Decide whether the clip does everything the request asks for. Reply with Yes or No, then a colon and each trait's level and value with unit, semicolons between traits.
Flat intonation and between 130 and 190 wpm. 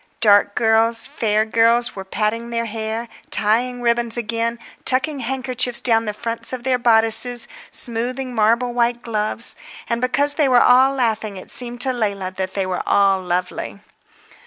Yes: narrow, 2.3 semitones; average, 160 wpm